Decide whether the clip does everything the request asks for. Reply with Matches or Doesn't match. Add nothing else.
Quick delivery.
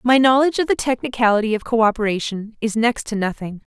Doesn't match